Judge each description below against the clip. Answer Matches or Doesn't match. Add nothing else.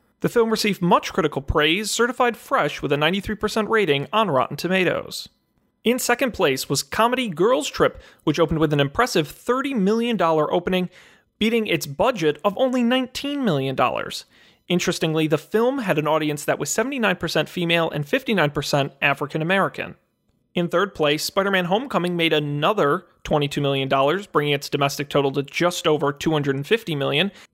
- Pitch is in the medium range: Matches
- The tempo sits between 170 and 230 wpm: Doesn't match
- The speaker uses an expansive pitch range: Matches